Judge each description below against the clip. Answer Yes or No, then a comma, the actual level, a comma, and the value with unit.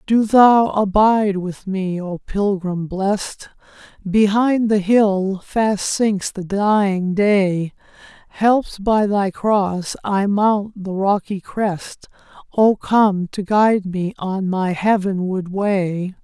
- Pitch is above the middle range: Yes, high, 200 Hz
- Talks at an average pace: No, slow, 125 wpm